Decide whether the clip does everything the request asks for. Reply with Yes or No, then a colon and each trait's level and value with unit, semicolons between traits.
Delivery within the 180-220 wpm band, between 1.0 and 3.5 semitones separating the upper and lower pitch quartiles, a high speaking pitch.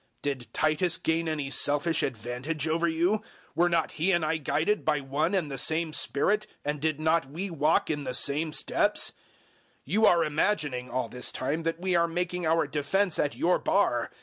No: average, 190 wpm; average, 2.9 semitones; medium, 160 Hz